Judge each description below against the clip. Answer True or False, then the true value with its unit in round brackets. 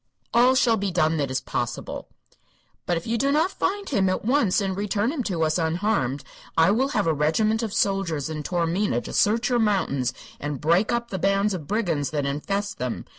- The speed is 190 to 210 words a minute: True (205 wpm)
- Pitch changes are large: True (5.8 semitones)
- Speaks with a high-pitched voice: True (195 Hz)